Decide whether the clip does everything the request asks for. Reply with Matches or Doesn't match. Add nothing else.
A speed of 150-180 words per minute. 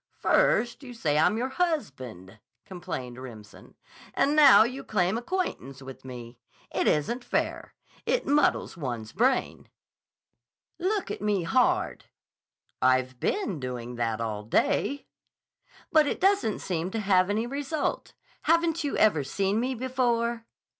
Doesn't match